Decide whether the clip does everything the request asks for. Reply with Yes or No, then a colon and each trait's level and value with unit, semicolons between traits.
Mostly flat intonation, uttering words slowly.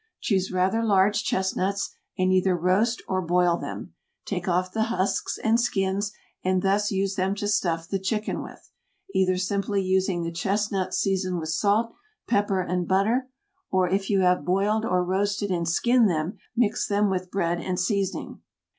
No: narrow, 1.9 semitones; average, 165 wpm